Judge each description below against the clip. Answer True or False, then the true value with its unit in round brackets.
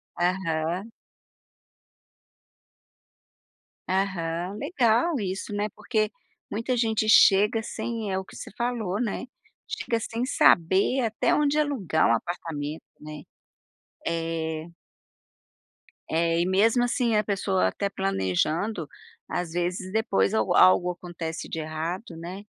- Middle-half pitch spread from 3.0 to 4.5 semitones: False (5.1 semitones)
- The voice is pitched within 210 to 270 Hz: False (190 Hz)